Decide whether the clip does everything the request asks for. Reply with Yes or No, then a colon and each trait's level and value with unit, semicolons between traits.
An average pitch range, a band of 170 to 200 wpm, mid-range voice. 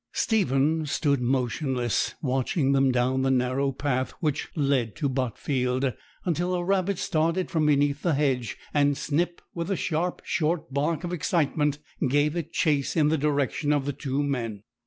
No: average, 3.4 semitones; average, 160 wpm; medium, 145 Hz